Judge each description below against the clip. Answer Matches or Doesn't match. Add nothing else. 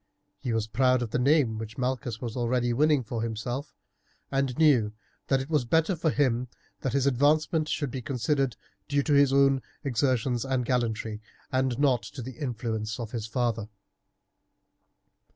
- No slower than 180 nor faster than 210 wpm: Doesn't match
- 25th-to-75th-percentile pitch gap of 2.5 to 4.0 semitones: Matches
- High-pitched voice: Doesn't match